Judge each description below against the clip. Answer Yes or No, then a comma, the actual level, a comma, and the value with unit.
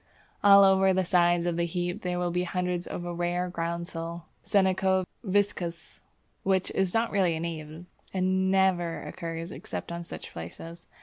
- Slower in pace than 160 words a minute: No, average, 165 wpm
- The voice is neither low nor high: Yes, medium, 175 Hz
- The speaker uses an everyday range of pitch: No, narrow, 1.8 semitones